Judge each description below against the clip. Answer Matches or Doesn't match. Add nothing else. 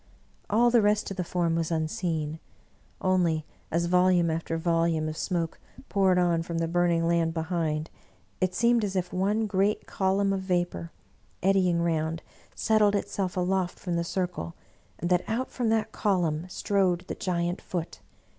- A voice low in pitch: Doesn't match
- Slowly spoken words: Doesn't match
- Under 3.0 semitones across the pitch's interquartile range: Matches